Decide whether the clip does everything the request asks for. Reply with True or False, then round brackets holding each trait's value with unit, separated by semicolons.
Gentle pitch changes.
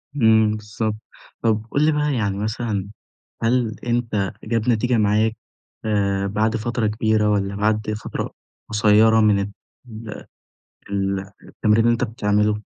True (1.6 semitones)